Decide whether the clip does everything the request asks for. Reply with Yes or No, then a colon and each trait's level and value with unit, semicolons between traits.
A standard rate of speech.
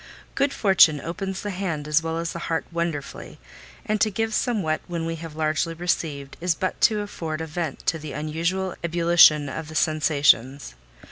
Yes: average, 180 wpm